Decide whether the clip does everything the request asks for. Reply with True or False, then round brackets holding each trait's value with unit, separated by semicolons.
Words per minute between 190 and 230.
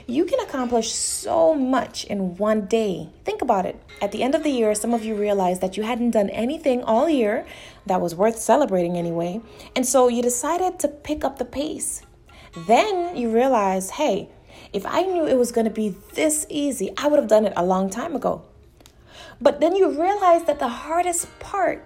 True (200 wpm)